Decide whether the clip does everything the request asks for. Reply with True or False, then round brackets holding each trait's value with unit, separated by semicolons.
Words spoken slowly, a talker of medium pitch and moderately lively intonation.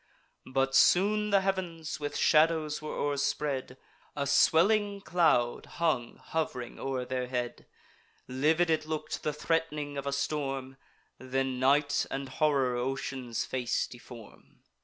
True (125 wpm; 145 Hz; 3.6 semitones)